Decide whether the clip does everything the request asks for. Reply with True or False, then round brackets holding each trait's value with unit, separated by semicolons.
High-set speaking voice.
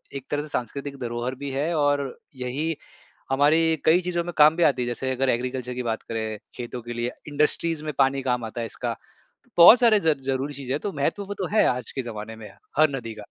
False (135 Hz)